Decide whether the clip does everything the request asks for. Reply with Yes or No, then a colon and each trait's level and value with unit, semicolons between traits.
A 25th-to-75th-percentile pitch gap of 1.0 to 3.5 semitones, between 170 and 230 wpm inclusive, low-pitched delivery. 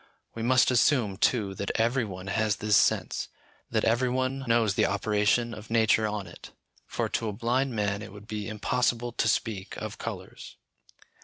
Yes: narrow, 2.5 semitones; average, 175 wpm; low, 110 Hz